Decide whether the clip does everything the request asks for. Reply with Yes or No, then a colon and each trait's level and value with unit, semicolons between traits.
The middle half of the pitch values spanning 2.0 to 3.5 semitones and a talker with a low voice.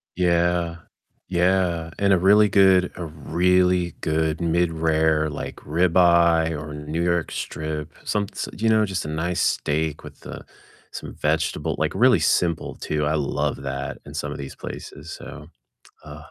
Yes: average, 2.8 semitones; very low, 85 Hz